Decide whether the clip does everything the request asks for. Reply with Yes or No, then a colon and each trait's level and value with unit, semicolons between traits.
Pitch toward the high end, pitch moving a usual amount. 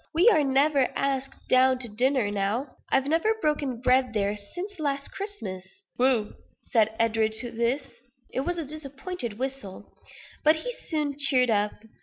Yes: very high, 265 Hz; average, 4.8 semitones